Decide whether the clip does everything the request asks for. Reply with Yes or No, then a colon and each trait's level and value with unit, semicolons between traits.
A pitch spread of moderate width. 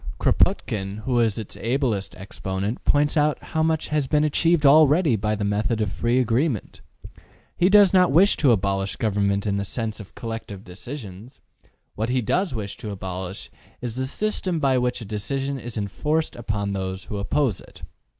No: wide, 6.2 semitones